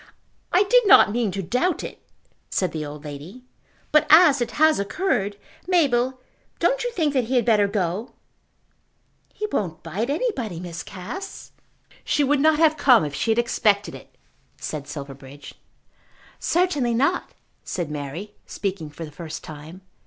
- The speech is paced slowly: No, average, 155 wpm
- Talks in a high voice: Yes, high, 220 Hz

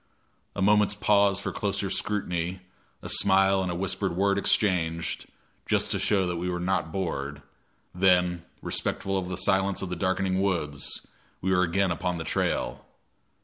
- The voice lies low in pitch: Yes, very low, 95 Hz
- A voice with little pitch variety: Yes, narrow, 1.9 semitones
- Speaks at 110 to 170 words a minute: Yes, average, 160 wpm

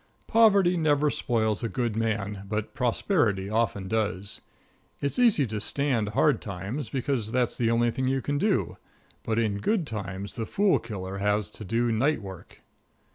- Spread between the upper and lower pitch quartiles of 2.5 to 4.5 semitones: No, average, 5.3 semitones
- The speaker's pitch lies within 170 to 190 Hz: No, low, 115 Hz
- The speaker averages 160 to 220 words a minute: Yes, average, 165 wpm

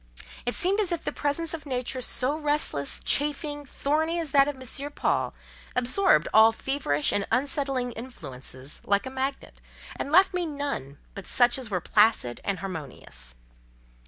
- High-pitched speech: Yes, very high, 265 Hz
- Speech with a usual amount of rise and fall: No, wide, 5.9 semitones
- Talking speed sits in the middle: Yes, average, 160 wpm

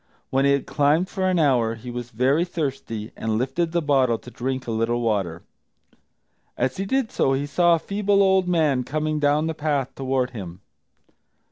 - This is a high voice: No, low, 135 Hz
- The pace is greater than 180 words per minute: Yes, average, 190 wpm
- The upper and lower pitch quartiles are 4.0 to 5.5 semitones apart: Yes, average, 5.0 semitones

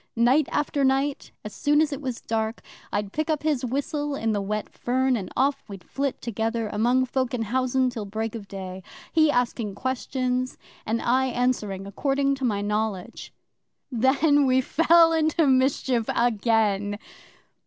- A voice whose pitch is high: Yes, very high, 250 Hz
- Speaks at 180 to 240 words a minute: No, average, 160 wpm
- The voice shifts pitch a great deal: No, average, 3.9 semitones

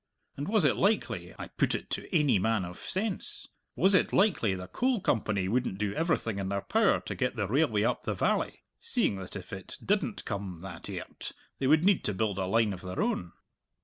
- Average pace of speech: No, fast, 215 wpm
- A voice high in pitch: No, low, 110 Hz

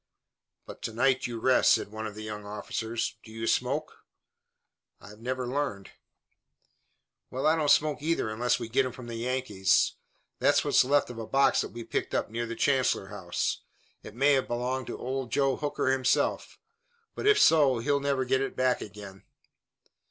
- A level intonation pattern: No, average, 3.4 semitones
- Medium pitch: No, low, 125 Hz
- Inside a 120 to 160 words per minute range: No, average, 180 wpm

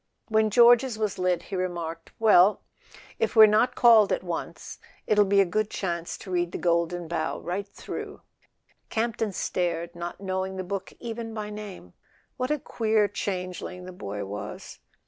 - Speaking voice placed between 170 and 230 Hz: Yes, high, 190 Hz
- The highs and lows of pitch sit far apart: No, average, 3.7 semitones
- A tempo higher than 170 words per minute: No, average, 165 wpm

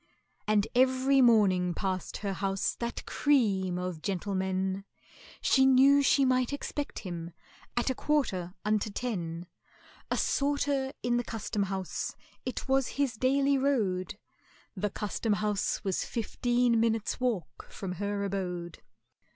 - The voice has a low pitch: No, high, 215 Hz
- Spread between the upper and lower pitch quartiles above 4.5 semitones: Yes, average, 5.3 semitones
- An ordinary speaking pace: No, slow, 130 wpm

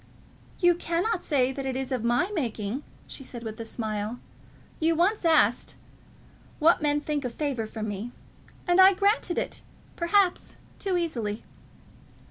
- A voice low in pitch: No, very high, 290 Hz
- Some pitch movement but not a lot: No, wide, 6.7 semitones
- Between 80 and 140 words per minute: No, average, 150 wpm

